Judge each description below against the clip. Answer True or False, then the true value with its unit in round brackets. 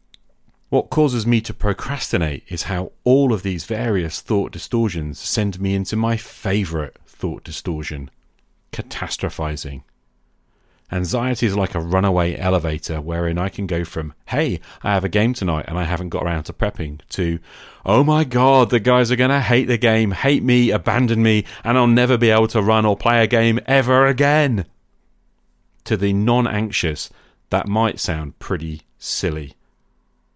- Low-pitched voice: True (100 Hz)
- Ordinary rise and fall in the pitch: False (6.0 semitones)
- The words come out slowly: False (160 wpm)